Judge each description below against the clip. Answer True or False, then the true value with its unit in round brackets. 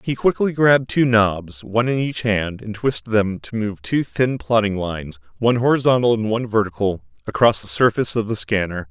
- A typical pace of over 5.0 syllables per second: True (5.5 syllables/s)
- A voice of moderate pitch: False (110 Hz)